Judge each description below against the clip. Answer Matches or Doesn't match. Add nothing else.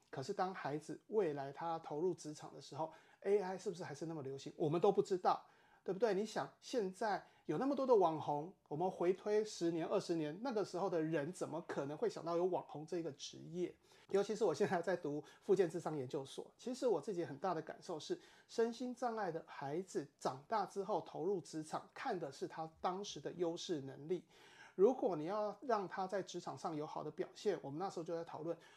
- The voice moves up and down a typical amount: Matches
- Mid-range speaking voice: Matches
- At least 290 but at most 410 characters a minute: Matches